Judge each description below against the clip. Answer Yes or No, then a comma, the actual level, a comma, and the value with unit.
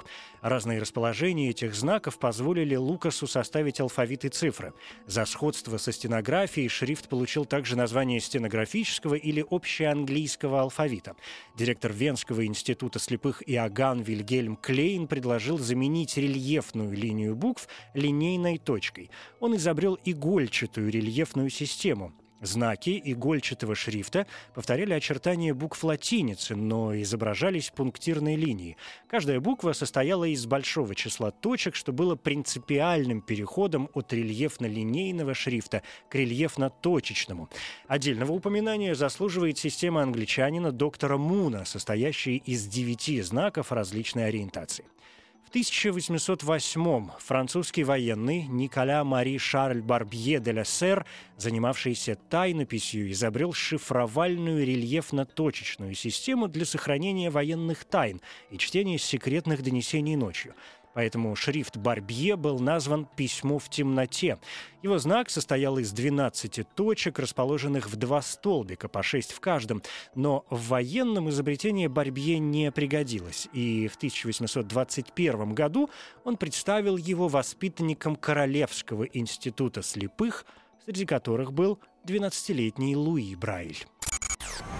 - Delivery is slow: Yes, slow, 105 wpm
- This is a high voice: No, medium, 140 Hz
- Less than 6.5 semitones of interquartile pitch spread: Yes, average, 5.3 semitones